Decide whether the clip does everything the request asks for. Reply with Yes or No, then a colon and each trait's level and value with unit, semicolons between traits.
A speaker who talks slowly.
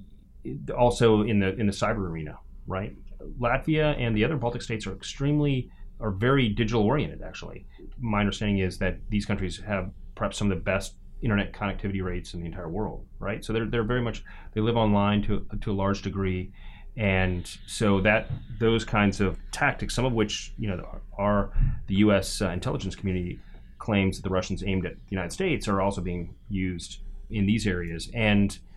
No: average, 185 wpm